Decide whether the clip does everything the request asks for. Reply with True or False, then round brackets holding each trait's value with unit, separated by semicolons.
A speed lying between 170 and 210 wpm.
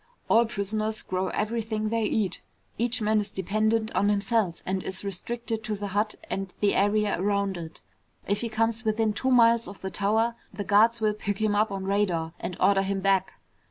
True (195 wpm)